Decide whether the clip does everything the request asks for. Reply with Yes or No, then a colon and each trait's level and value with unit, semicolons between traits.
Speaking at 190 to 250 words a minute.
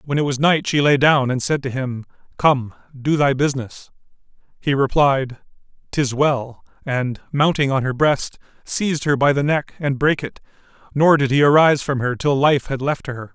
Yes: average, 195 wpm